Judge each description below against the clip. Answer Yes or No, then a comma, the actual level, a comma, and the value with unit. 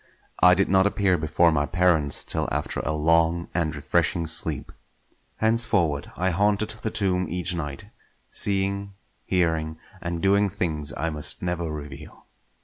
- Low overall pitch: Yes, very low, 85 Hz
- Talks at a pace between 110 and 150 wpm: Yes, average, 140 wpm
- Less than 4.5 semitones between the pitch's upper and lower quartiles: Yes, average, 3.8 semitones